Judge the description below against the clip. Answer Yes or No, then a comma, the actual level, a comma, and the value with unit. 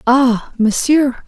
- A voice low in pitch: No, very high, 255 Hz